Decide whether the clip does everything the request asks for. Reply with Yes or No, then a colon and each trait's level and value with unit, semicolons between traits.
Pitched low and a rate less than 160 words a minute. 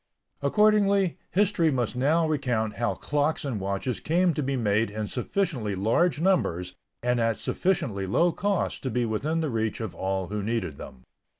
No: low, 125 Hz; average, 170 wpm